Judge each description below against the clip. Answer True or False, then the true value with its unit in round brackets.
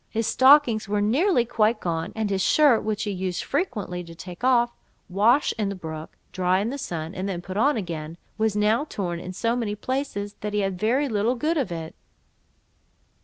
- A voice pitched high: True (210 Hz)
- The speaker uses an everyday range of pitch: True (4.7 semitones)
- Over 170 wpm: True (200 wpm)